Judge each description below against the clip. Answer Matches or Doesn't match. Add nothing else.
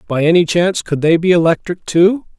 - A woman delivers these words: Doesn't match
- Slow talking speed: Doesn't match